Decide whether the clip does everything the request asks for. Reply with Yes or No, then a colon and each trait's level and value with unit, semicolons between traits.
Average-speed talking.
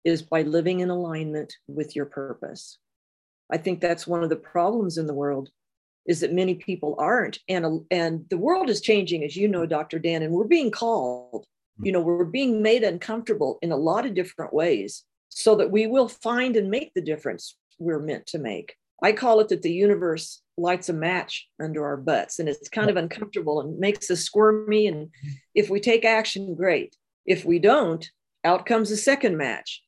Yes: average, 195 wpm